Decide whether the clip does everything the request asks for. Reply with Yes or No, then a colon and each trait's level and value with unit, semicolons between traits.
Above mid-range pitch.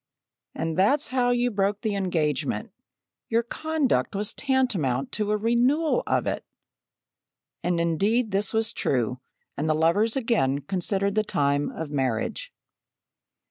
Yes: high, 200 Hz